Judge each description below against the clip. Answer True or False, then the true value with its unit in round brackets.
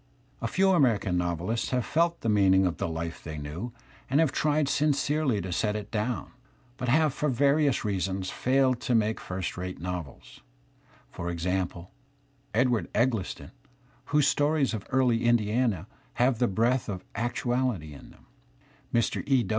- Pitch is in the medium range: False (115 Hz)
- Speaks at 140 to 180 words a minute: True (160 wpm)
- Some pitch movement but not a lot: False (6.0 semitones)